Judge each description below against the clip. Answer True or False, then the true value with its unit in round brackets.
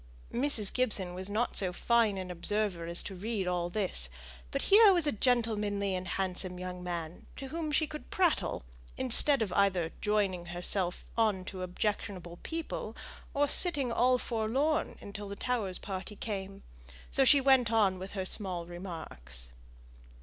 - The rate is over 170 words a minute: False (155 wpm)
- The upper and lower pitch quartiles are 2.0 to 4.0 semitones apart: False (5.1 semitones)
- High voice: True (200 Hz)